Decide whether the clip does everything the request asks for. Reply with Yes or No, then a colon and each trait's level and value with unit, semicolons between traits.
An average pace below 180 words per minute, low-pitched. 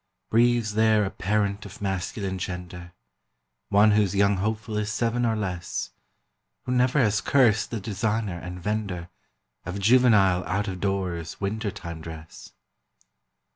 Yes: slow, 135 wpm; low, 100 Hz